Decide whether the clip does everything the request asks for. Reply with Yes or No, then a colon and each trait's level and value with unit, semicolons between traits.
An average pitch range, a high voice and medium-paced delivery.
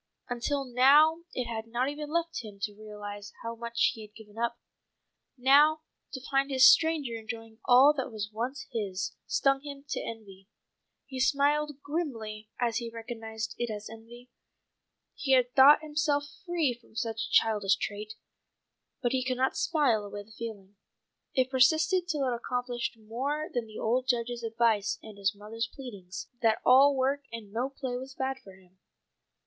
Yes: average, 3.7 semitones; high, 240 Hz; average, 170 wpm